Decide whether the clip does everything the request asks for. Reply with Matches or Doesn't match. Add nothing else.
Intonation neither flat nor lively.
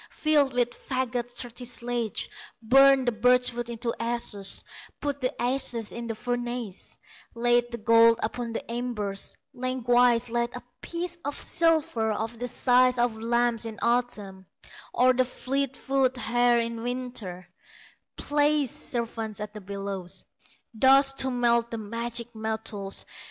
Doesn't match